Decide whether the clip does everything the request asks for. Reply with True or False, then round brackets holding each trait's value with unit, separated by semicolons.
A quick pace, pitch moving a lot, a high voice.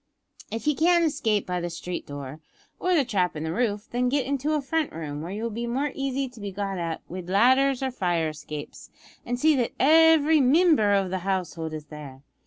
True (215 wpm; 7.9 semitones; 220 Hz)